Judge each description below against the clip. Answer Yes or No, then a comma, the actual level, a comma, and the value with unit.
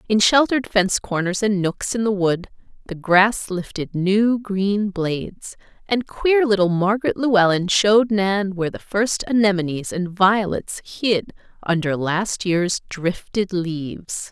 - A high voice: Yes, high, 195 Hz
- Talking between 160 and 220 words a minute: No, average, 145 wpm